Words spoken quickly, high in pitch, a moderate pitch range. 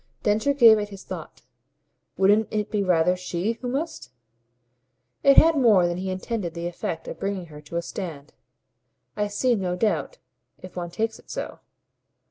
No: average, 170 wpm; high, 200 Hz; average, 4.2 semitones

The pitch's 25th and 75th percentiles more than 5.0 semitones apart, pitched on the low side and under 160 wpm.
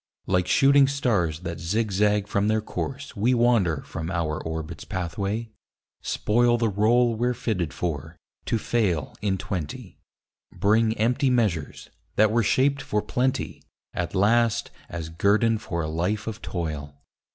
Yes: wide, 5.4 semitones; low, 105 Hz; average, 145 wpm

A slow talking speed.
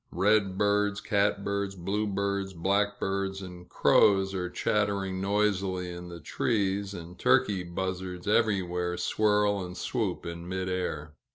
Yes: slow, 115 wpm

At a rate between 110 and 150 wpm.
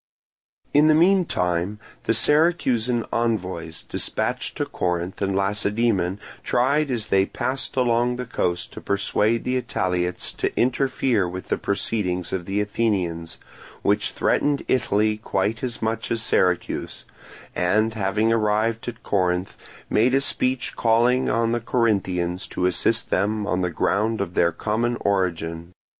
Yes: average, 140 wpm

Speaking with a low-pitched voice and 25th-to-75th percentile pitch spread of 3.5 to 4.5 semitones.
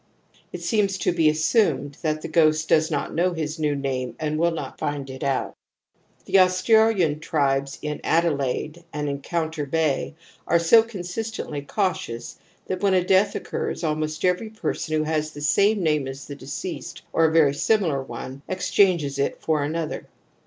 No: medium, 155 Hz; average, 3.8 semitones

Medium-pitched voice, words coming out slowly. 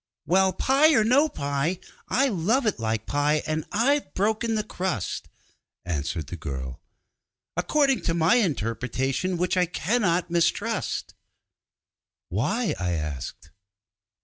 Yes: medium, 175 Hz; slow, 120 wpm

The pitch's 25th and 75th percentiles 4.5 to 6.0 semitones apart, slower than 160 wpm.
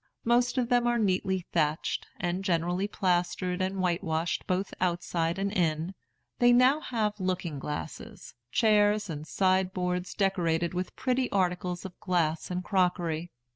No: average, 3.0 semitones; average, 140 wpm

